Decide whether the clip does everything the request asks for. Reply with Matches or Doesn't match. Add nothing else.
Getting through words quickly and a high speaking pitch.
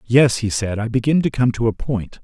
Doesn't match